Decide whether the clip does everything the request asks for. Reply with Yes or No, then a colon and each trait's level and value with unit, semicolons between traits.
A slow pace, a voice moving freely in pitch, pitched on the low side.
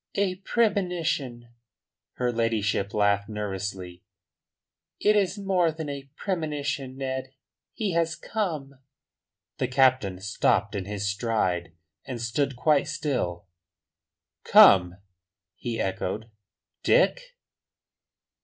Yes: slow, 100 wpm; wide, 8.1 semitones; low, 130 Hz